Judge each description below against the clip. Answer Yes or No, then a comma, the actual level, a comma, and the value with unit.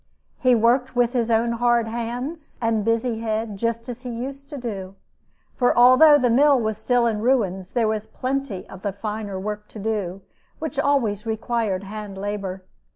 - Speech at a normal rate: Yes, average, 175 wpm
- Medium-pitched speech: No, high, 230 Hz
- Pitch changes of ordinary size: Yes, average, 3.0 semitones